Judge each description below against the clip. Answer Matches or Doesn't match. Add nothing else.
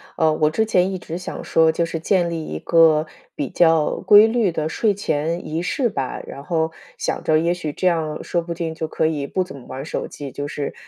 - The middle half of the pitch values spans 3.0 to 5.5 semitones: Doesn't match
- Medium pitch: Matches